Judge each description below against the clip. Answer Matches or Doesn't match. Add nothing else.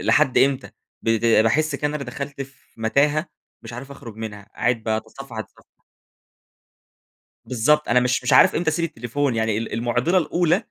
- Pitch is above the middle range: Doesn't match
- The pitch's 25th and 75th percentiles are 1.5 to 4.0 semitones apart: Doesn't match